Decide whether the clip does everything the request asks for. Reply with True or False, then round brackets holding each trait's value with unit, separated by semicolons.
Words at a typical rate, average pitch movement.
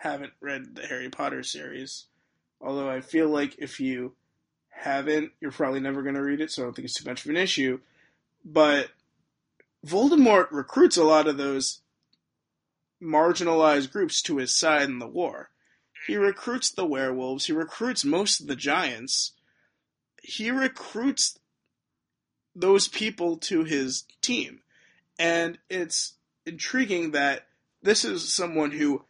False (145 wpm; 5.8 semitones)